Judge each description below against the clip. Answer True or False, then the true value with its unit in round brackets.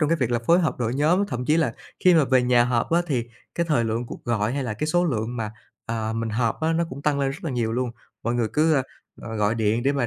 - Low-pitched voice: True (125 Hz)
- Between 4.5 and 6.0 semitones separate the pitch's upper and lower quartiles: True (4.8 semitones)